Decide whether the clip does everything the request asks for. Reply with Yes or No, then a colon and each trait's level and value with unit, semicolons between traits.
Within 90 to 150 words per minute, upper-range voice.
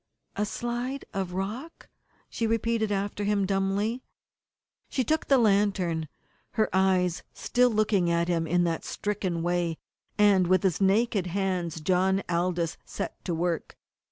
Yes: average, 140 wpm; high, 195 Hz